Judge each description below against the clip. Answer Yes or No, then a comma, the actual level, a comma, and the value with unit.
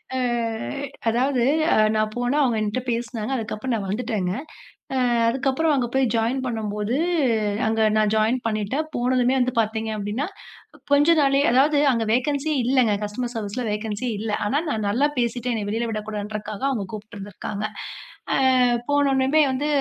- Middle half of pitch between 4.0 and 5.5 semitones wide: No, average, 3.5 semitones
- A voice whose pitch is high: Yes, high, 235 Hz